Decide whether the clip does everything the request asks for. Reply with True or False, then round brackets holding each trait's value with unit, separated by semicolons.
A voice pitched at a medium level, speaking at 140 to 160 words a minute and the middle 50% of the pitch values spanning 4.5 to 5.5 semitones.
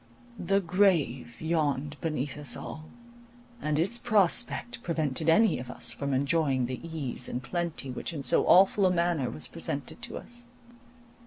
True (160 Hz; 155 wpm; 5.1 semitones)